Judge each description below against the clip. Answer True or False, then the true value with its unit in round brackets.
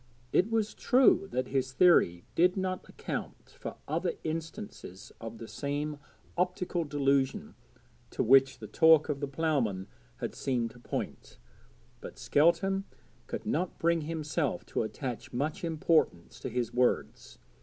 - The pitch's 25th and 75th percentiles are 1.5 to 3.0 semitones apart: False (5.1 semitones)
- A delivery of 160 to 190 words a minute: False (140 wpm)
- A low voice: False (150 Hz)